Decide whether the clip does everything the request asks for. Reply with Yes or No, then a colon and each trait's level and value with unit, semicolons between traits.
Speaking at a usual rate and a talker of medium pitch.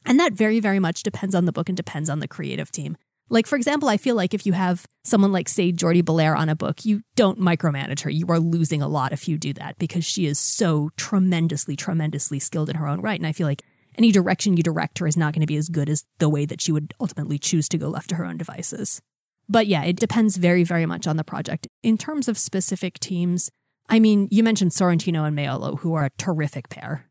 No: fast, 250 wpm; medium, 170 Hz